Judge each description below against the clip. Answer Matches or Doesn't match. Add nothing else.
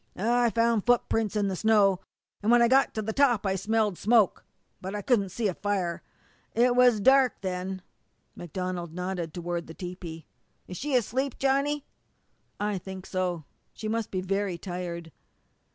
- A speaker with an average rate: Matches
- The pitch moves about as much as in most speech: Matches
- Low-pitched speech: Doesn't match